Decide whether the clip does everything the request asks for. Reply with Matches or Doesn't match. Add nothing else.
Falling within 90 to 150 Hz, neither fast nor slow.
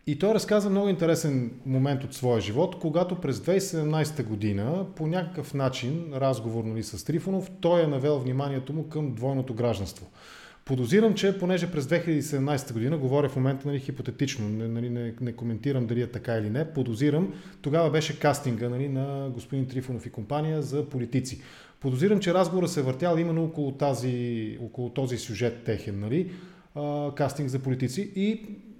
Matches